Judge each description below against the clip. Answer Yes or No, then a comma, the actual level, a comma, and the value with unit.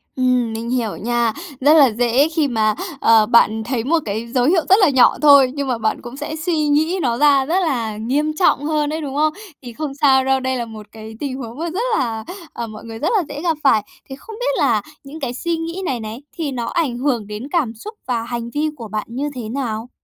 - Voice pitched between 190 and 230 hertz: No, very high, 260 Hz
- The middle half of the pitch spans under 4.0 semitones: No, average, 4.5 semitones